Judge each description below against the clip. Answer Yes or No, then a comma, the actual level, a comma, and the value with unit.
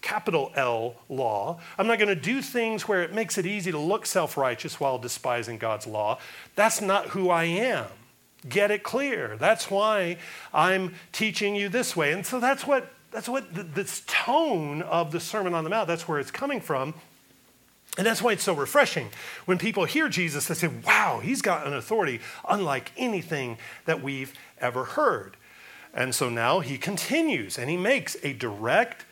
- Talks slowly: No, average, 185 wpm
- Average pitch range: No, wide, 5.8 semitones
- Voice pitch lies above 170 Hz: Yes, high, 190 Hz